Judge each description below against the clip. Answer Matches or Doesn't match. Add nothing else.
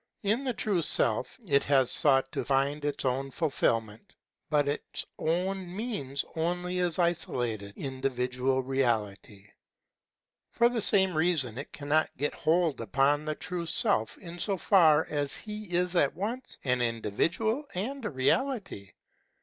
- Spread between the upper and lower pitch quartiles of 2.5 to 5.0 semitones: Doesn't match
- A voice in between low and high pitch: Matches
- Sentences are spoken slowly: Doesn't match